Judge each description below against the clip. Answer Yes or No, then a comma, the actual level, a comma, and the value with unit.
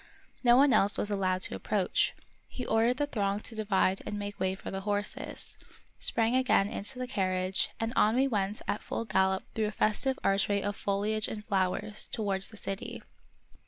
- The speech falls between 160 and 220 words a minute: Yes, average, 185 wpm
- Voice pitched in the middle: No, high, 205 Hz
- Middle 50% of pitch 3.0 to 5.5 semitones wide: No, narrow, 2.5 semitones